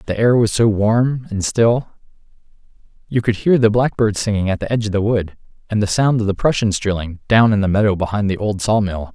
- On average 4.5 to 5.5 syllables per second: No, 5.7 syllables/s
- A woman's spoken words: No, male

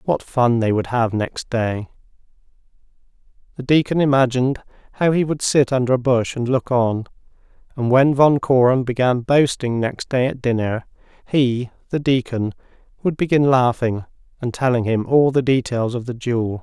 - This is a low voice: Yes, low, 125 Hz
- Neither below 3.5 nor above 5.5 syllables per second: Yes, 4.8 syllables/s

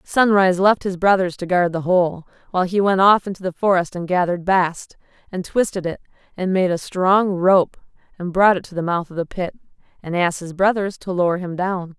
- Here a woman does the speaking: Yes, female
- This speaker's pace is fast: Yes, fast, 215 wpm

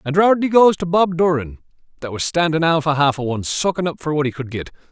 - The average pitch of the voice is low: No, medium, 155 Hz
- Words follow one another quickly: Yes, fast, 255 wpm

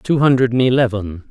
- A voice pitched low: Yes, low, 120 Hz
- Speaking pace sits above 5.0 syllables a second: No, 4.7 syllables/s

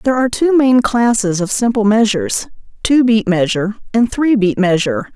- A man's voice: No, female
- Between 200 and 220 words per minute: No, average, 175 wpm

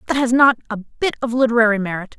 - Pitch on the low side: No, high, 235 Hz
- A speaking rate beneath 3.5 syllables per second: No, 6.6 syllables/s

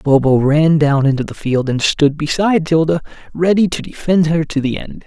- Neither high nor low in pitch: Yes, medium, 155 Hz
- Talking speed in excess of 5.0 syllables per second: Yes, 5.2 syllables/s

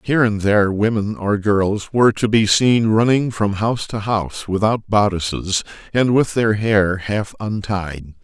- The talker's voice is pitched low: Yes, low, 105 Hz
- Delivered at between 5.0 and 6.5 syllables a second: No, 4.4 syllables/s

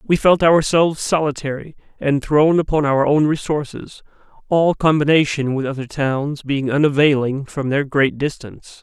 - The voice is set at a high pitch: No, medium, 145 Hz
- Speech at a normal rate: Yes, average, 145 wpm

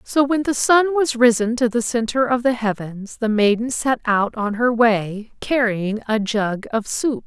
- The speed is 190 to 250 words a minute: Yes, average, 200 wpm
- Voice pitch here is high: Yes, high, 235 Hz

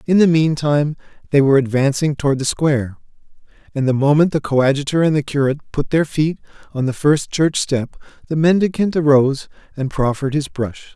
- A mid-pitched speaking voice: Yes, medium, 145 Hz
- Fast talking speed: No, average, 175 wpm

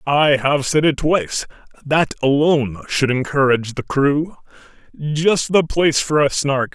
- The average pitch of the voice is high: No, medium, 145 Hz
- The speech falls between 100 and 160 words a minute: Yes, average, 150 wpm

